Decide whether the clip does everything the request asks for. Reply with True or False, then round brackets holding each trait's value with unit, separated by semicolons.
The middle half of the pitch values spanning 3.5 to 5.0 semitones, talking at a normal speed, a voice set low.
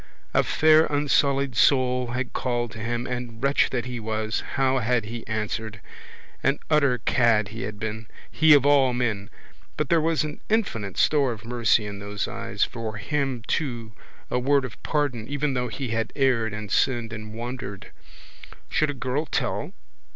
True (3.8 semitones; 175 wpm; 125 Hz)